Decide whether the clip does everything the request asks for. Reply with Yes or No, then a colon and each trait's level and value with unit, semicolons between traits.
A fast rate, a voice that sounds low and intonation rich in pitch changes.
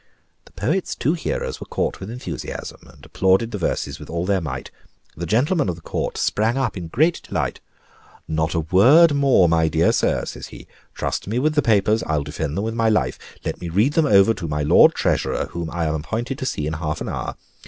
Yes: fast, 220 wpm; very low, 95 Hz; wide, 7.1 semitones